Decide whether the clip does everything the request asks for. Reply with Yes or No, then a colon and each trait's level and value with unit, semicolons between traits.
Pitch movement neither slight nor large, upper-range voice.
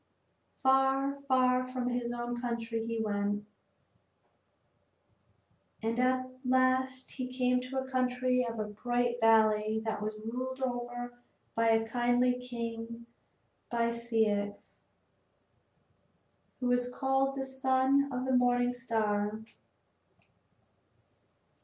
No: narrow, 2.0 semitones; high, 245 Hz